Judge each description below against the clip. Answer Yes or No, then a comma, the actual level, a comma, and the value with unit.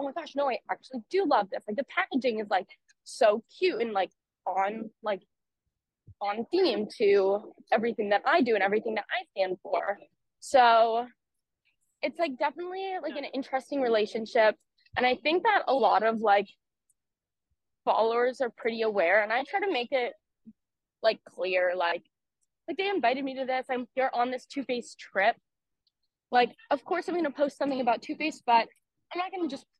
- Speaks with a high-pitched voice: Yes, very high, 250 Hz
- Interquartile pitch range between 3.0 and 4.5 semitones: No, average, 5.2 semitones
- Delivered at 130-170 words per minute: No, average, 180 wpm